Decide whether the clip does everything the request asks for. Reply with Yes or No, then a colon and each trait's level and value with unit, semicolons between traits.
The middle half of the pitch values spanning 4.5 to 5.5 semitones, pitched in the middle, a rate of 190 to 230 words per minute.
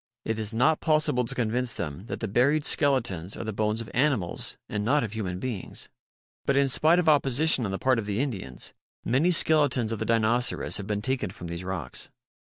No: average, 5.1 semitones; low, 115 Hz; fast, 205 wpm